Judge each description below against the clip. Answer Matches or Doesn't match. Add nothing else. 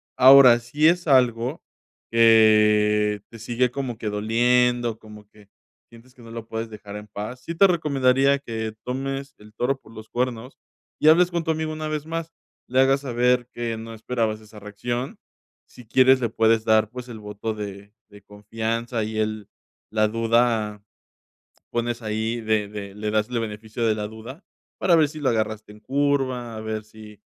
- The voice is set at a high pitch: Doesn't match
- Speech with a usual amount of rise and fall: Matches